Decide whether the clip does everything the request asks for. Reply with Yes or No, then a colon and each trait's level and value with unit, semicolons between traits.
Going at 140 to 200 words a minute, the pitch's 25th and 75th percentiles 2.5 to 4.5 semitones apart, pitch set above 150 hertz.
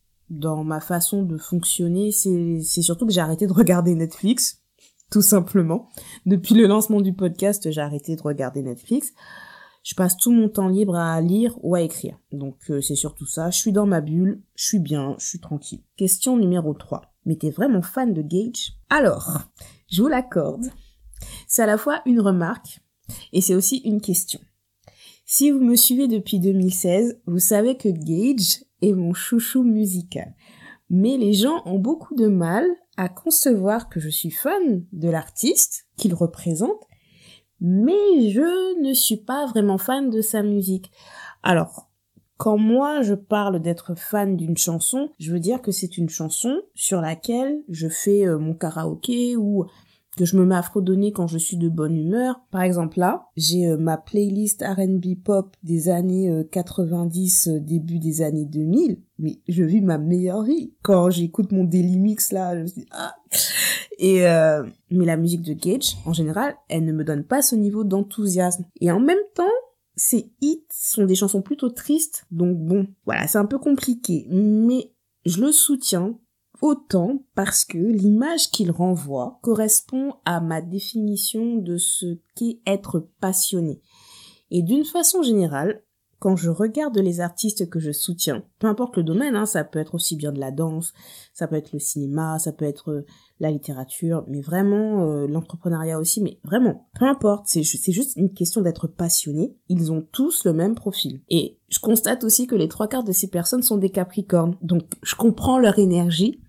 No: average, 180 wpm; average, 5.1 semitones; high, 190 Hz